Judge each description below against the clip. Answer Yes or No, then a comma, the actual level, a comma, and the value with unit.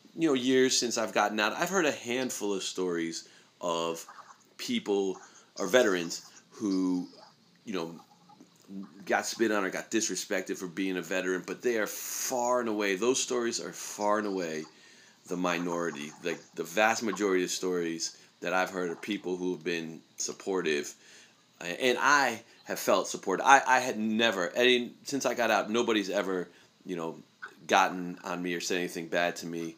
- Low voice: Yes, very low, 95 Hz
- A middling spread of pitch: Yes, average, 4.1 semitones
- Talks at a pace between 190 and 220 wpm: No, average, 175 wpm